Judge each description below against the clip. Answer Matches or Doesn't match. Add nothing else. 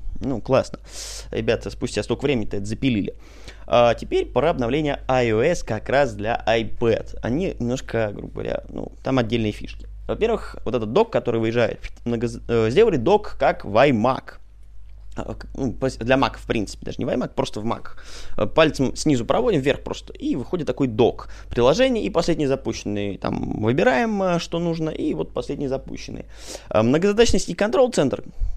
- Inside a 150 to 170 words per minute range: Matches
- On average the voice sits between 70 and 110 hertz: Doesn't match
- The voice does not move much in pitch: Doesn't match